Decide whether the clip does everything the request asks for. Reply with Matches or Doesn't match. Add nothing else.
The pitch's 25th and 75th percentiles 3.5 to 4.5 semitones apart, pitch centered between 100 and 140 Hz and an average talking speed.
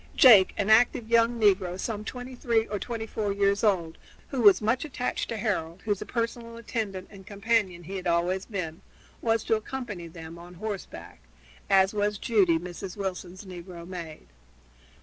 Doesn't match